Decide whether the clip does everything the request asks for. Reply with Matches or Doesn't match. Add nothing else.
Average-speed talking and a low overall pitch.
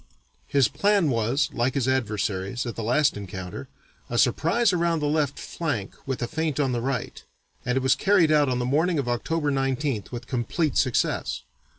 Matches